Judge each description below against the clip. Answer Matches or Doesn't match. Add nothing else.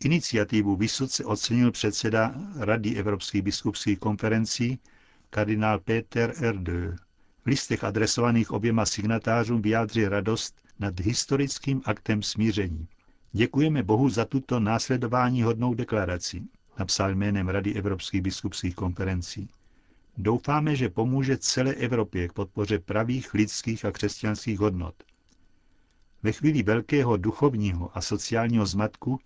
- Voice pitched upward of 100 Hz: Matches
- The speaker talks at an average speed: Doesn't match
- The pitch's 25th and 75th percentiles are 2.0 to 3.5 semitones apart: Matches